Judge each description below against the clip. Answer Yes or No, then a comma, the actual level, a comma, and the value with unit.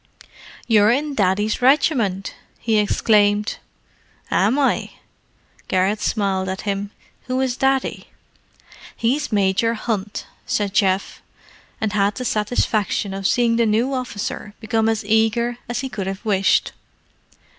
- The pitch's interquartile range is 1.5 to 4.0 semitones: Yes, average, 3.0 semitones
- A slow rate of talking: Yes, slow, 125 wpm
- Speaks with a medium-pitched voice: No, high, 215 Hz